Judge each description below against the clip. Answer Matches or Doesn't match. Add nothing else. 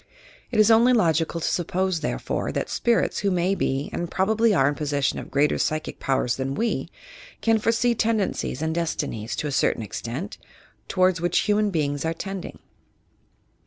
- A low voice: Doesn't match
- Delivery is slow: Doesn't match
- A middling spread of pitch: Doesn't match